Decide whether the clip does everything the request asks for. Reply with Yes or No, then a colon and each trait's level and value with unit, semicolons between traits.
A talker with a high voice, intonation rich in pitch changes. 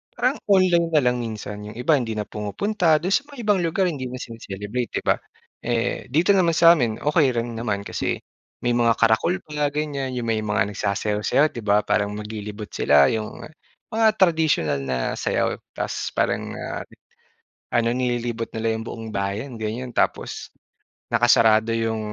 No: low, 120 Hz; wide, 6.1 semitones